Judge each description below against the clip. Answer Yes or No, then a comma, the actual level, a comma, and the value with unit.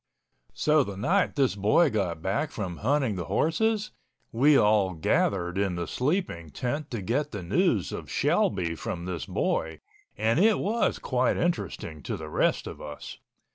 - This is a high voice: No, low, 105 Hz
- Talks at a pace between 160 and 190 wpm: Yes, average, 165 wpm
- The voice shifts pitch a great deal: Yes, wide, 9.0 semitones